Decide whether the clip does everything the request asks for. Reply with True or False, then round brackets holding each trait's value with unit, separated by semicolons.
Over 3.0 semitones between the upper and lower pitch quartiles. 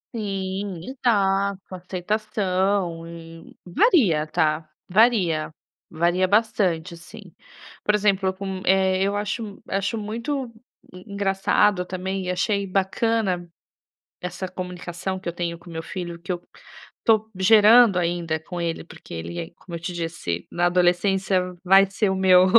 False (2.5 semitones)